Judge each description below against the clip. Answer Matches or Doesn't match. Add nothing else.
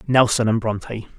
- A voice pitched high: Doesn't match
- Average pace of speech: Matches